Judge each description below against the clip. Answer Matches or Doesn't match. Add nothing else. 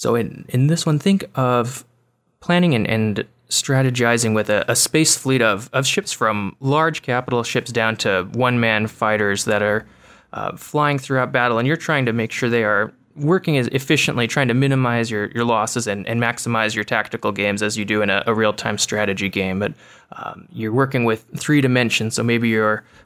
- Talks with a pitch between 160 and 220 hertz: Doesn't match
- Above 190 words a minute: Matches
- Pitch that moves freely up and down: Doesn't match